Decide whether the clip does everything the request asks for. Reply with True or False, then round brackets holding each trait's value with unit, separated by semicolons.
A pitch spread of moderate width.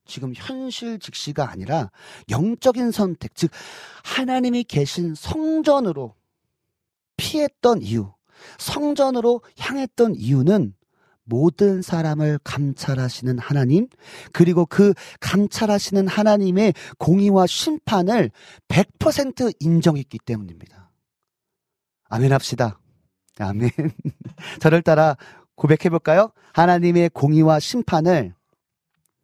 False (7.6 semitones)